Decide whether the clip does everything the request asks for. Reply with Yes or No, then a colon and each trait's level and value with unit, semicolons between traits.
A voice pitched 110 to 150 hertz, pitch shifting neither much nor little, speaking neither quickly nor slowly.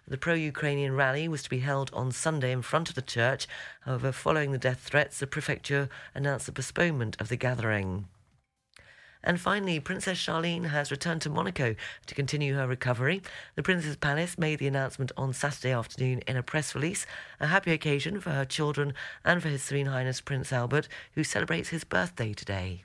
Yes: medium, 140 Hz; average, 3.3 semitones; average, 185 wpm